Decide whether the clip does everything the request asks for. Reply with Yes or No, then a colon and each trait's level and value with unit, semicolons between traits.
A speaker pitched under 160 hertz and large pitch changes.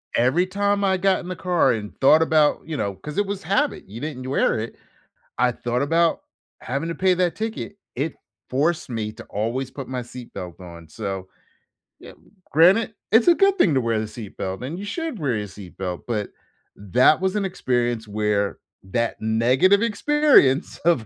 Yes: low, 135 Hz; wide, 8.9 semitones